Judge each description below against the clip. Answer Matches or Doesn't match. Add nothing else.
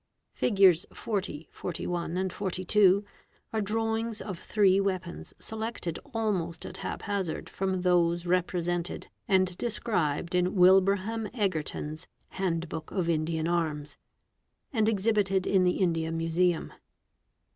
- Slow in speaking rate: Matches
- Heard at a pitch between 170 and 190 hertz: Matches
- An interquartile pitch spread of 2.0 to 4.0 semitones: Matches